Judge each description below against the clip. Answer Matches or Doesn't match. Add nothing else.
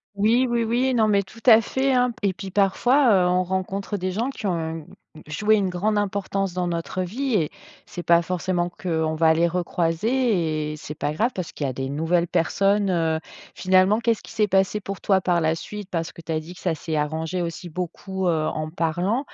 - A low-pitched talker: Doesn't match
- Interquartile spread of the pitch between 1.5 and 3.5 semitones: Doesn't match